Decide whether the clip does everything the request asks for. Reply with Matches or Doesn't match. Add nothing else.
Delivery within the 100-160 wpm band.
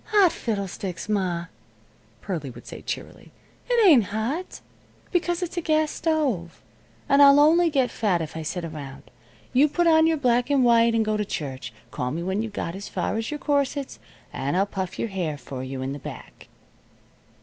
Doesn't match